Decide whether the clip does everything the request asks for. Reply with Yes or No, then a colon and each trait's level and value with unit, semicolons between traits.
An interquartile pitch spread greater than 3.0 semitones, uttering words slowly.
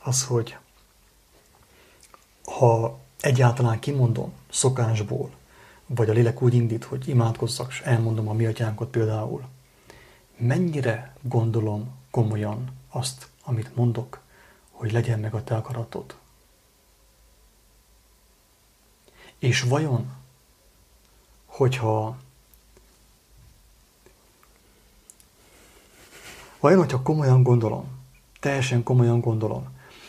No: narrow, 2.4 semitones; slow, 80 wpm